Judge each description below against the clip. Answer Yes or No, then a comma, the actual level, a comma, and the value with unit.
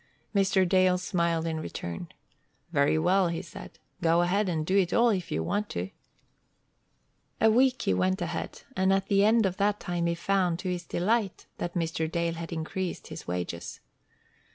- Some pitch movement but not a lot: Yes, average, 3.1 semitones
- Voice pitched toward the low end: No, medium, 175 Hz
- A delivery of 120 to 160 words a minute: No, average, 175 wpm